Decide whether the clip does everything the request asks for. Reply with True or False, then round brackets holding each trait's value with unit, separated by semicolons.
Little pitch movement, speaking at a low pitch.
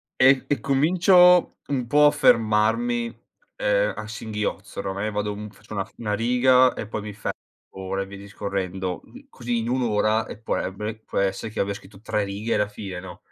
False (3.1 semitones; 105 Hz)